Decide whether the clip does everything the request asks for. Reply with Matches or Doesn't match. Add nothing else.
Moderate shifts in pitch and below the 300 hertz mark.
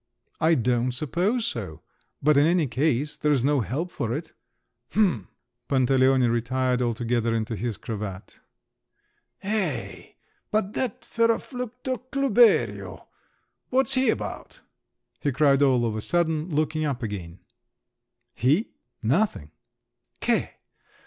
Doesn't match